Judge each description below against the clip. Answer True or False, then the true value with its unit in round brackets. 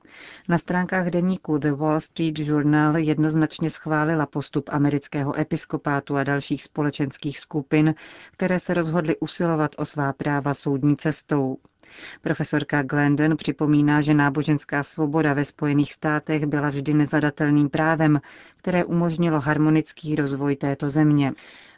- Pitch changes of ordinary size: False (1.4 semitones)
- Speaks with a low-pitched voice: False (150 Hz)